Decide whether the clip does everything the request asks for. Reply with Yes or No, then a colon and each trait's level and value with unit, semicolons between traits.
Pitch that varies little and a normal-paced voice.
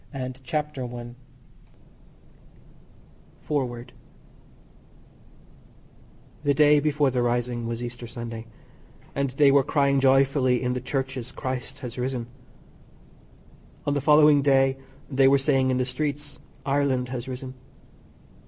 No: narrow, 2.1 semitones; slow, 115 wpm